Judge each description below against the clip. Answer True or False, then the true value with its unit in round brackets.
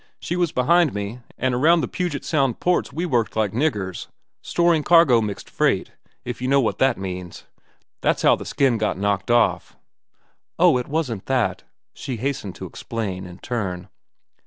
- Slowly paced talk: False (165 wpm)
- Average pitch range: False (6.2 semitones)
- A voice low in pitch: True (125 Hz)